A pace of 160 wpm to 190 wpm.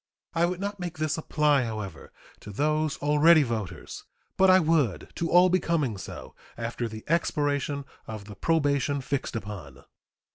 No: average, 150 wpm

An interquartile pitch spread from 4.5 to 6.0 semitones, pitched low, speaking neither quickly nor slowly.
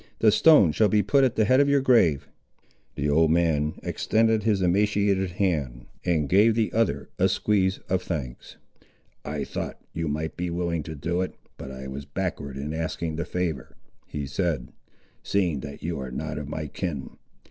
Yes: wide, 5.5 semitones; very low, 85 Hz; average, 180 wpm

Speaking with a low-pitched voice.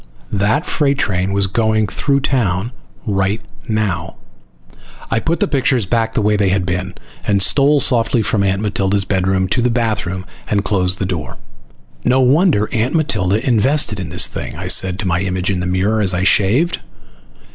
Yes: low, 105 Hz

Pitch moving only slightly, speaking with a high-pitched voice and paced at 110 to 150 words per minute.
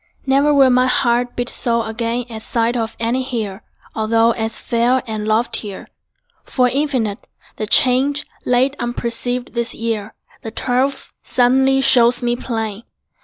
Yes: narrow, 2.0 semitones; high, 240 Hz; average, 140 wpm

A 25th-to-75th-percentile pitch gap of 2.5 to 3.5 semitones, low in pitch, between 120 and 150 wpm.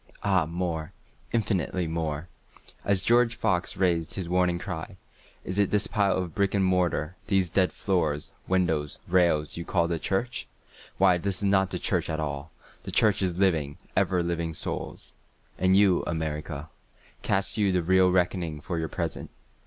Yes: average, 2.9 semitones; very low, 90 Hz; average, 140 wpm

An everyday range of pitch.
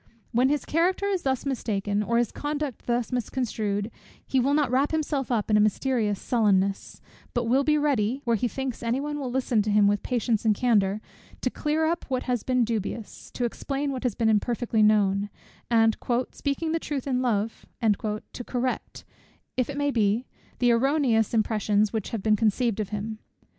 Yes: average, 4.0 semitones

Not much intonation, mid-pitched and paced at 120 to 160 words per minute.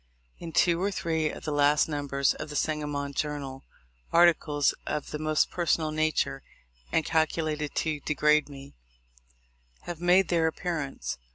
Yes: narrow, 1.9 semitones; medium, 155 Hz; average, 150 wpm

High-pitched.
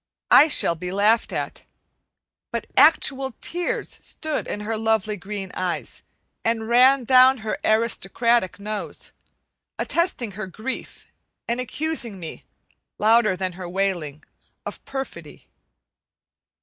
Yes: high, 220 Hz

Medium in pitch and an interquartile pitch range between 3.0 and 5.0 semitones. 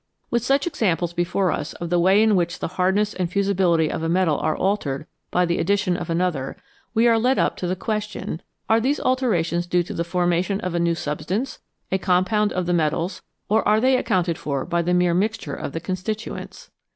Yes: medium, 180 Hz; average, 3.6 semitones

